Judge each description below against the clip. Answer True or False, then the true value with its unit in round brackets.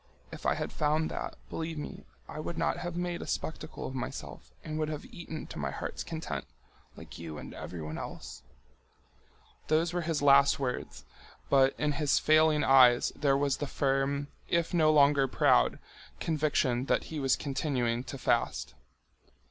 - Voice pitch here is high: False (145 Hz)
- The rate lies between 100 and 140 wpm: False (165 wpm)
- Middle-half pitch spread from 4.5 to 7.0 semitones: False (2.8 semitones)